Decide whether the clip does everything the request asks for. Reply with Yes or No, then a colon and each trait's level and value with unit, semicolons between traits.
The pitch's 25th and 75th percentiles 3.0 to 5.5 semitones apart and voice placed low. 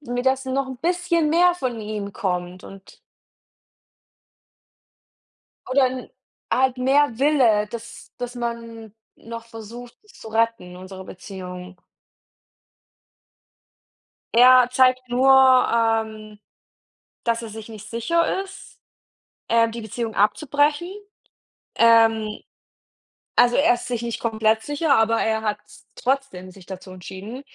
No: average, 3.3 semitones; high, 230 Hz